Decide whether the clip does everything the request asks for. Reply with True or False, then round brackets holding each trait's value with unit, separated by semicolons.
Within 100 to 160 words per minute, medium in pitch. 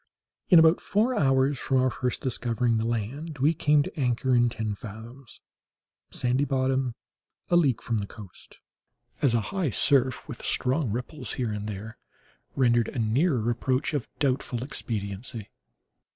False (150 wpm; 125 Hz)